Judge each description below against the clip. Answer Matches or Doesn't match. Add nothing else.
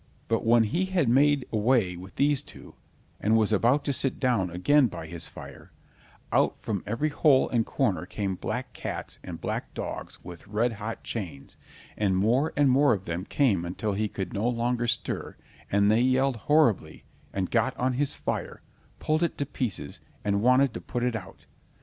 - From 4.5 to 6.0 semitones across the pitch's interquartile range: Matches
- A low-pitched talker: Matches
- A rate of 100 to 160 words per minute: Doesn't match